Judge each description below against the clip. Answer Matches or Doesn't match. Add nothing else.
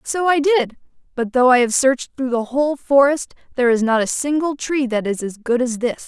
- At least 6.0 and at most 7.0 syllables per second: Doesn't match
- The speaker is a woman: Matches